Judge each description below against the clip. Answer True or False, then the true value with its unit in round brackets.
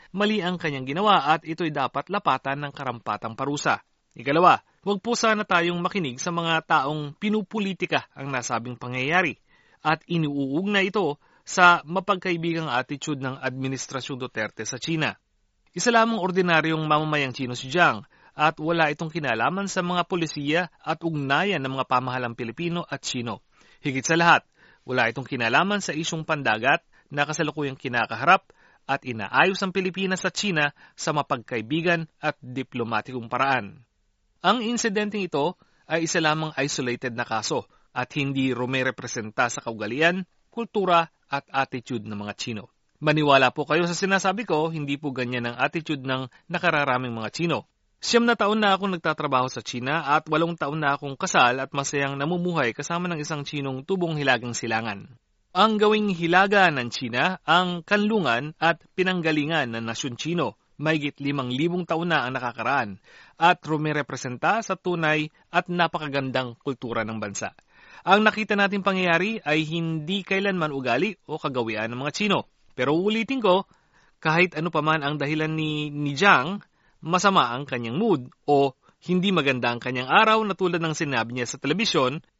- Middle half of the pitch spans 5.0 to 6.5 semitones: True (5.3 semitones)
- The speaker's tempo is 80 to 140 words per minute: False (155 wpm)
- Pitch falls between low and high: True (155 Hz)